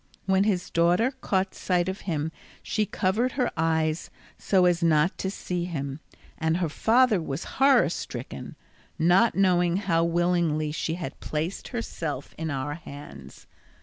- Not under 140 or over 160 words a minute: Yes, average, 150 wpm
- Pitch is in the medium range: Yes, medium, 175 Hz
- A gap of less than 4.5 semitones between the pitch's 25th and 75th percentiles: Yes, average, 3.4 semitones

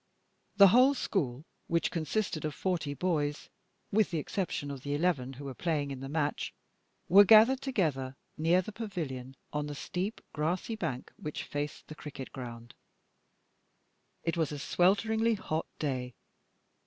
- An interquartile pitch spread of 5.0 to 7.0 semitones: Yes, average, 5.3 semitones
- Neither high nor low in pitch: Yes, medium, 155 Hz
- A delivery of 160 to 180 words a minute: No, average, 150 wpm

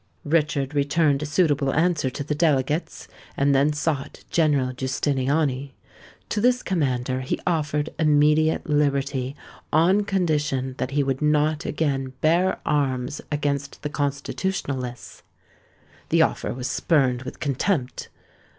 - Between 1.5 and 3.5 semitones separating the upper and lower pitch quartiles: Yes, narrow, 2.6 semitones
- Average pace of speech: No, slow, 125 wpm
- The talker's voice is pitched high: No, medium, 145 Hz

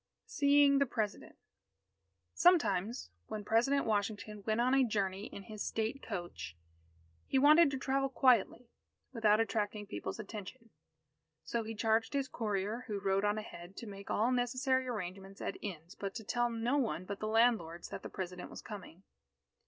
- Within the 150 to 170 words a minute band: Yes, average, 165 wpm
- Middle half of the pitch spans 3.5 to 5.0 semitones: Yes, average, 3.8 semitones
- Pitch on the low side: No, high, 220 Hz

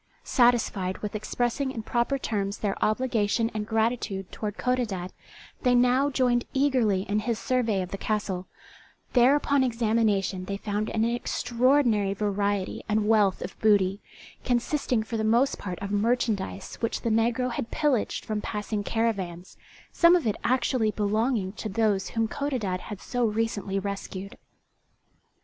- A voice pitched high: Yes, high, 220 Hz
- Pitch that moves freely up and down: No, average, 3.2 semitones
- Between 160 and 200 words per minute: No, average, 145 wpm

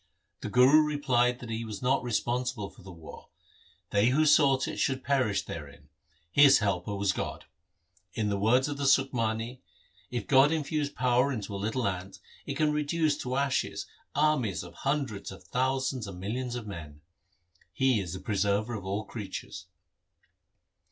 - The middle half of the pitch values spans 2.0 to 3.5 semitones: No, average, 5.1 semitones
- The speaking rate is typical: Yes, average, 165 wpm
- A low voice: Yes, low, 120 Hz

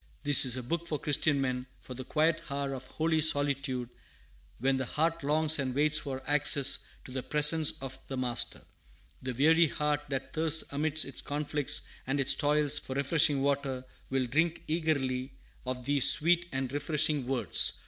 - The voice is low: No, medium, 145 Hz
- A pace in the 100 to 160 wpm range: No, average, 170 wpm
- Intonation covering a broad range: No, narrow, 2.6 semitones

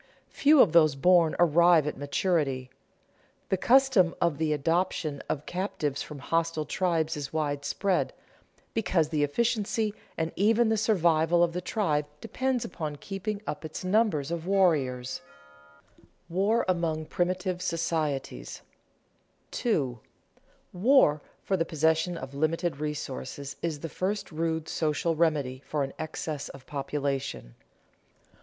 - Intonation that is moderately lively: Yes, average, 3.8 semitones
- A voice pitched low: No, medium, 165 Hz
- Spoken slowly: Yes, slow, 130 wpm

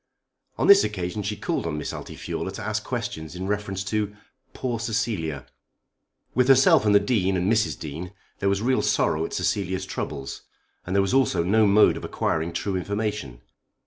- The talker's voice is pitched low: Yes, low, 100 Hz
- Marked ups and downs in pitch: No, average, 3.5 semitones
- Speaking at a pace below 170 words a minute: No, average, 175 wpm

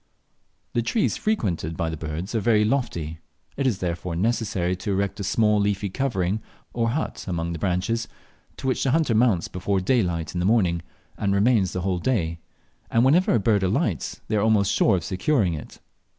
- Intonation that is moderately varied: Yes, average, 4.6 semitones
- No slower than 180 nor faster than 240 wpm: Yes, average, 190 wpm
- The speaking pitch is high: No, low, 100 Hz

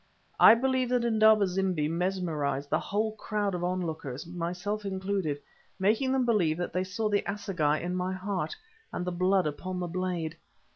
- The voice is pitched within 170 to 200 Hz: Yes, medium, 185 Hz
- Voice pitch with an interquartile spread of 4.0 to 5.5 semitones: No, average, 3.2 semitones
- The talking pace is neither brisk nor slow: Yes, average, 165 wpm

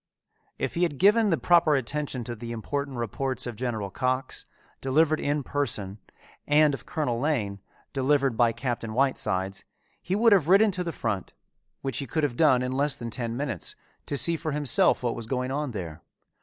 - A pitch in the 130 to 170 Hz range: Yes, low, 135 Hz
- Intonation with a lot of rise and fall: No, average, 4.2 semitones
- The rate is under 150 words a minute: No, average, 185 wpm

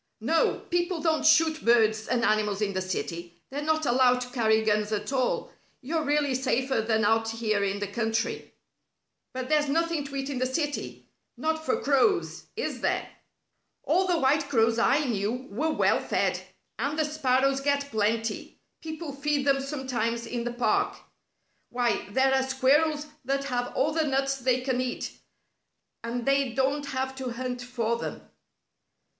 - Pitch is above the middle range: Yes, very high, 260 Hz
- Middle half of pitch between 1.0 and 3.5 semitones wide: No, average, 3.9 semitones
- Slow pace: No, average, 165 wpm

